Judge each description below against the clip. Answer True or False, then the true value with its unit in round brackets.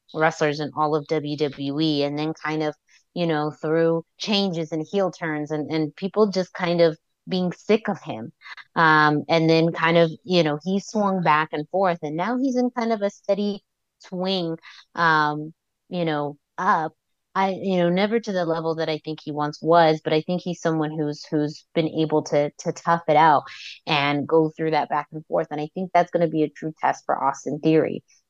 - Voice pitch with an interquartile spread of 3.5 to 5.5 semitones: False (2.8 semitones)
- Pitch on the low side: False (160 Hz)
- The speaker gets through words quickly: True (210 wpm)